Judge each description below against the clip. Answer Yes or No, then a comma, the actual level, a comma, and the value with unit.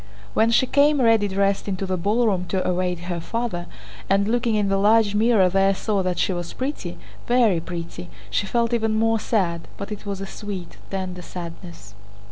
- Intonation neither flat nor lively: Yes, average, 3.7 semitones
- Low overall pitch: No, high, 200 Hz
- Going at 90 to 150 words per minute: No, average, 185 wpm